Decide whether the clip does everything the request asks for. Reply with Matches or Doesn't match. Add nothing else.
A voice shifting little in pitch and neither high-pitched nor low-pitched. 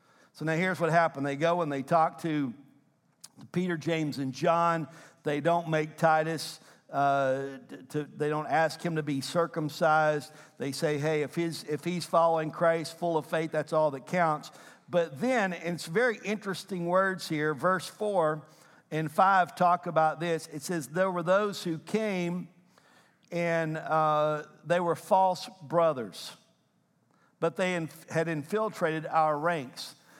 Matches